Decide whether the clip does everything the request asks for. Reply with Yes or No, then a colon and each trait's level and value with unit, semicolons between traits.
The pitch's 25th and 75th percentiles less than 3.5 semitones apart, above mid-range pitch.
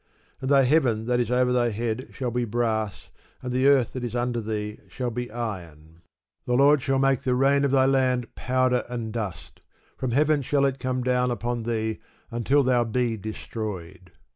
No: average, 2.7 semitones; low, 125 Hz